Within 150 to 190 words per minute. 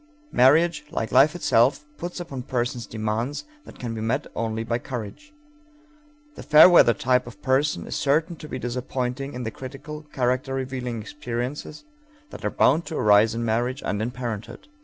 Yes: average, 170 wpm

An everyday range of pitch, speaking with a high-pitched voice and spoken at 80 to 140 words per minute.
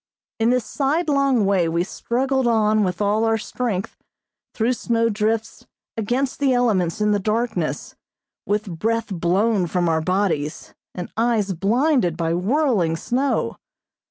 Yes: average, 4.9 semitones; high, 215 Hz; slow, 135 wpm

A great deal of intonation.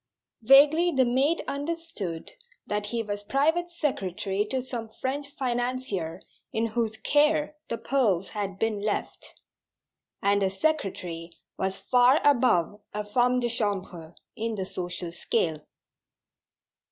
Yes: wide, 5.8 semitones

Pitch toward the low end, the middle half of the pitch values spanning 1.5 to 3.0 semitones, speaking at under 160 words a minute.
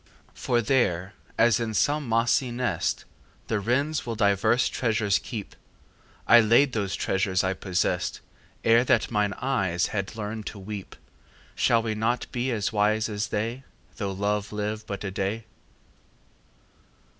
Yes: low, 110 Hz; average, 2.7 semitones; average, 145 wpm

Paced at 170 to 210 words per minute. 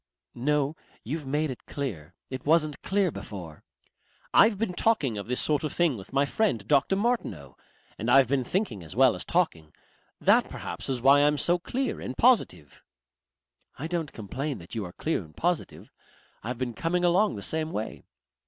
Yes: average, 180 wpm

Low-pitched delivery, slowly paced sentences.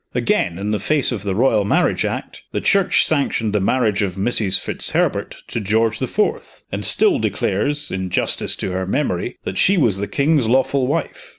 No: low, 110 Hz; average, 190 wpm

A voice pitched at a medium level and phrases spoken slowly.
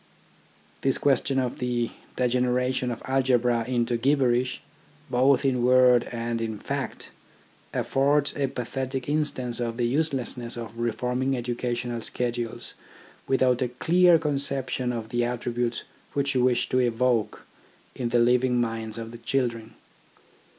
No: low, 125 Hz; slow, 130 wpm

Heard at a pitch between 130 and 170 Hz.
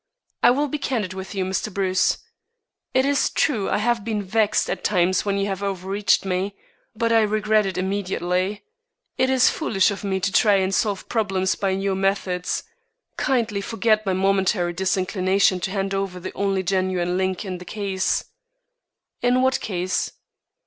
No: high, 195 Hz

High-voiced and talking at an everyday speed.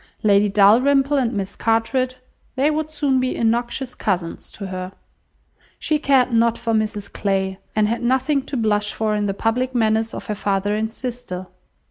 Yes: high, 225 Hz; average, 165 wpm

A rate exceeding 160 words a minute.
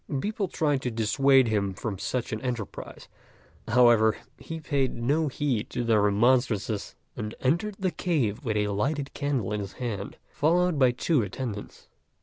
No: average, 155 wpm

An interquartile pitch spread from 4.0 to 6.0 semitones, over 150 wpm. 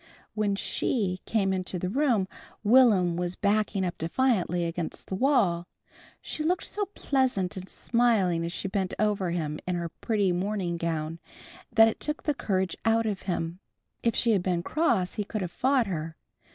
Yes: average, 4.4 semitones; average, 175 wpm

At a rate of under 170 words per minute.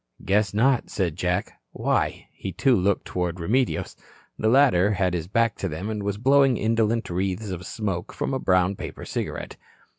No: average, 175 wpm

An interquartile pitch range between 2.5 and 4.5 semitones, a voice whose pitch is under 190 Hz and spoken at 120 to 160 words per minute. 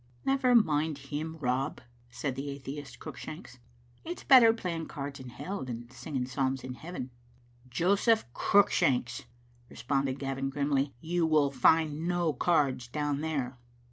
Yes: average, 3.7 semitones; medium, 140 Hz; average, 145 wpm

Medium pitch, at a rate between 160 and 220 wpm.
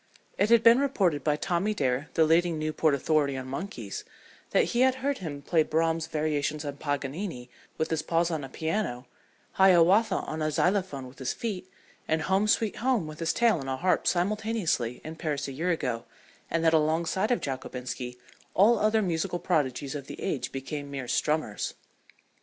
Yes: medium, 160 Hz; average, 180 wpm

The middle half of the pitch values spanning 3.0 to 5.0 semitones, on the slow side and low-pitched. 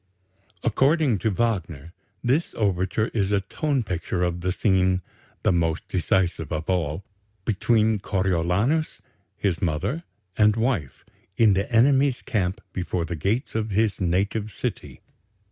Yes: average, 4.1 semitones; slow, 130 wpm; low, 100 Hz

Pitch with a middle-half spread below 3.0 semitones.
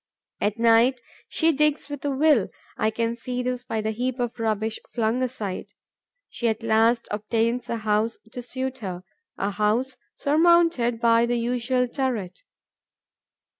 Yes: narrow, 2.6 semitones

